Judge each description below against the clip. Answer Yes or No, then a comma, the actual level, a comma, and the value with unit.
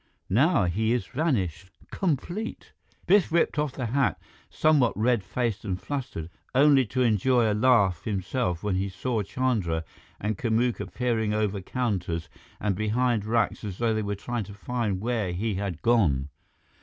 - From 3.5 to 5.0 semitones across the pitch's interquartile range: Yes, average, 4.4 semitones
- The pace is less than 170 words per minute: Yes, average, 155 wpm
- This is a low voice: Yes, low, 110 Hz